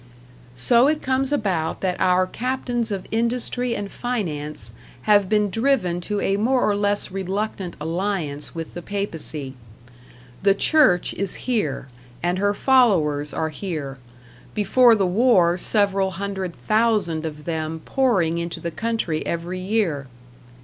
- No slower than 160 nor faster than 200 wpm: No, slow, 135 wpm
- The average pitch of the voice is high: Yes, high, 195 Hz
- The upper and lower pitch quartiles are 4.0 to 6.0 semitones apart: Yes, average, 5.0 semitones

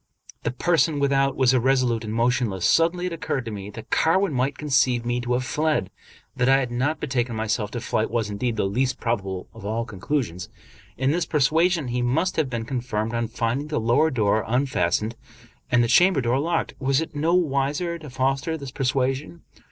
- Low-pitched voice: Yes, low, 130 Hz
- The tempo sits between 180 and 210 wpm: Yes, average, 190 wpm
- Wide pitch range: No, average, 4.1 semitones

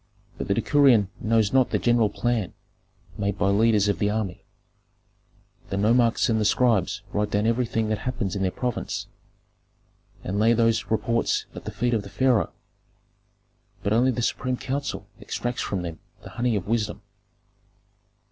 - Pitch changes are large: No, average, 2.8 semitones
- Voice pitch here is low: Yes, low, 110 Hz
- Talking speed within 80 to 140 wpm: No, average, 160 wpm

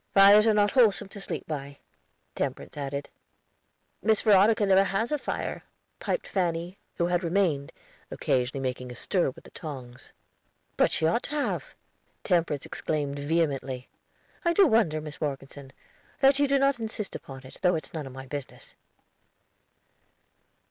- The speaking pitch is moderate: Yes, medium, 170 Hz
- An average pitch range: No, wide, 6.8 semitones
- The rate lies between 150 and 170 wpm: Yes, average, 155 wpm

